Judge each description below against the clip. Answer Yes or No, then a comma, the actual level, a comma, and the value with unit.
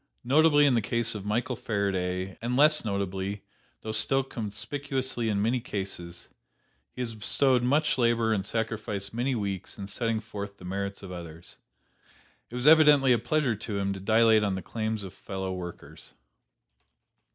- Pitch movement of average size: Yes, average, 4.0 semitones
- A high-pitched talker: No, low, 110 Hz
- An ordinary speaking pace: Yes, average, 165 wpm